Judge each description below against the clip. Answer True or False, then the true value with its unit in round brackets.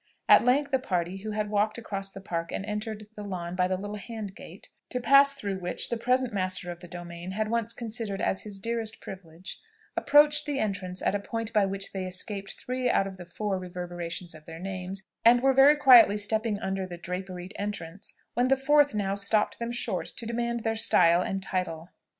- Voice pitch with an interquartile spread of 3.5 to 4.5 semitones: True (4.0 semitones)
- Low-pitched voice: False (205 Hz)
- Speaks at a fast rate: True (210 wpm)